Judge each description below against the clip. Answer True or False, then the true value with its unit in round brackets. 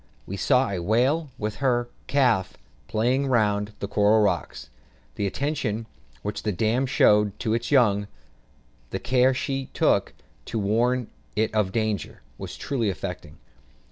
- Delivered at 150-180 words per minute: False (140 wpm)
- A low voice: True (110 Hz)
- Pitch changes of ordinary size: True (3.7 semitones)